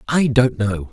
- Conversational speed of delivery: Yes, average, 195 wpm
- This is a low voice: Yes, low, 115 Hz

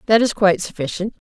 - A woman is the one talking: Yes, female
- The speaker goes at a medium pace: Yes, average, 190 wpm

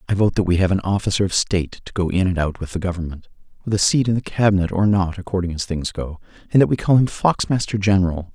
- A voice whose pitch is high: No, very low, 95 Hz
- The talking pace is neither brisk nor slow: No, fast, 250 wpm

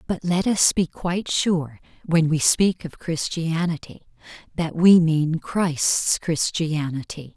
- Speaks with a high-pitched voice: No, medium, 165 Hz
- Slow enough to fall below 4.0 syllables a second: Yes, 3.6 syllables/s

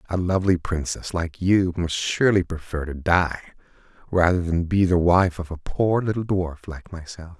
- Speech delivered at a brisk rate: No, average, 180 wpm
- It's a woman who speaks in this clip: No, male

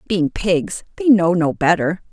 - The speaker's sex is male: No, female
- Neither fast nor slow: Yes, average, 170 wpm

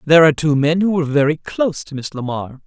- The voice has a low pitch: No, medium, 155 Hz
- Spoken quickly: Yes, fast, 245 wpm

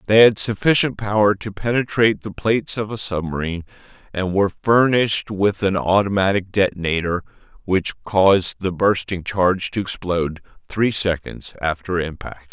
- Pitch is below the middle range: Yes, very low, 95 Hz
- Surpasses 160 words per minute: No, average, 140 wpm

